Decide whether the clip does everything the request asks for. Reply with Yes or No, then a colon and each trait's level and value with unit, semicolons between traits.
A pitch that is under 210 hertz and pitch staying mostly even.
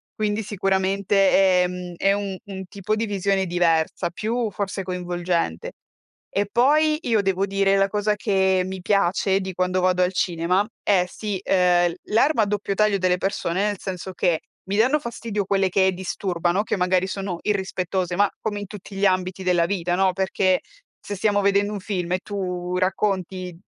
Yes: high, 190 Hz; narrow, 2.0 semitones